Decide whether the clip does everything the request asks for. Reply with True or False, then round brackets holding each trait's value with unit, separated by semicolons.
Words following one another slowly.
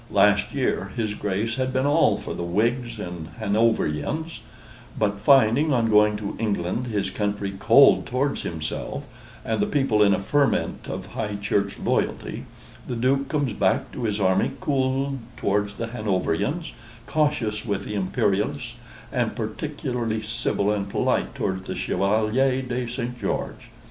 False (150 wpm)